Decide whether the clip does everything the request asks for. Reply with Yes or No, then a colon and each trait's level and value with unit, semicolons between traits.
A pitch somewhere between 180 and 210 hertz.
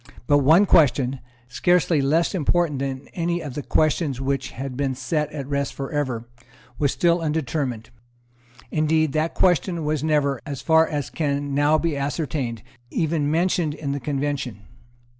No: medium, 145 Hz